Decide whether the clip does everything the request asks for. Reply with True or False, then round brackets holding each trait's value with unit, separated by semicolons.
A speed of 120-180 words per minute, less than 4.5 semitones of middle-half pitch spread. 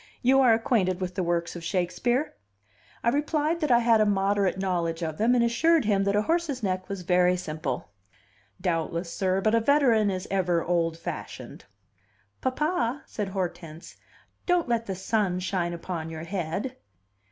False (165 wpm; 5.1 semitones)